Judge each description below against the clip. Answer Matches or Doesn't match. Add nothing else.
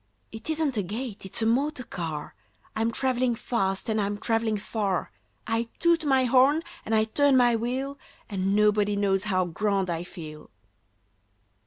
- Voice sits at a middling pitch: Doesn't match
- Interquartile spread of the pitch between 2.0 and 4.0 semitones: Doesn't match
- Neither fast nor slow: Matches